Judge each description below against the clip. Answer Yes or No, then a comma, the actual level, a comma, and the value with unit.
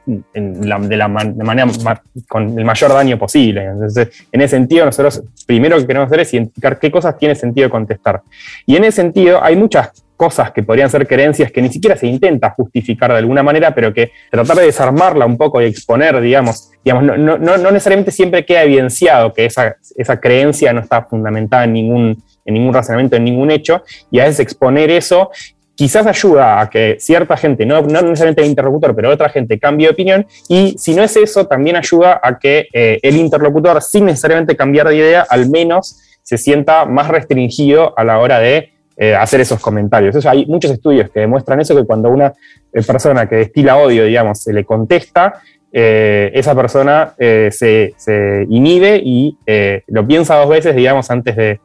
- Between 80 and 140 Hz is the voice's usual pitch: Yes, low, 135 Hz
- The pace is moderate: No, fast, 200 wpm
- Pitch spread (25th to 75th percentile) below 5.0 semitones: No, wide, 5.4 semitones